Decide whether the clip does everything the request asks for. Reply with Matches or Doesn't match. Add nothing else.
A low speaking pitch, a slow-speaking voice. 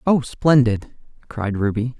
Matches